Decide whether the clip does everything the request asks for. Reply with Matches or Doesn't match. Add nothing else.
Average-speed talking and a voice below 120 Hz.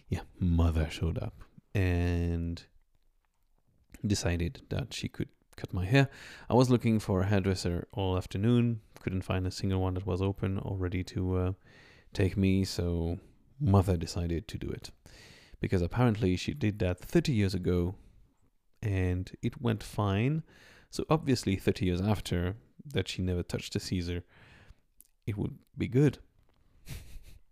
Matches